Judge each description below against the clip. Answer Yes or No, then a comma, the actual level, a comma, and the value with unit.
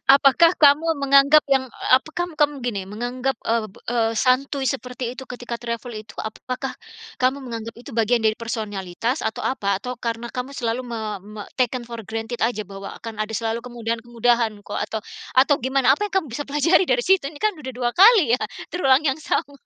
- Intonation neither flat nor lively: Yes, average, 3.3 semitones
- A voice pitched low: No, high, 245 Hz